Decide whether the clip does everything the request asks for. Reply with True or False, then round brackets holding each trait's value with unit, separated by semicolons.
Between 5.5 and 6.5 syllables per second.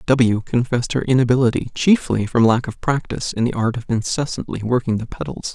True (5.7 syllables/s)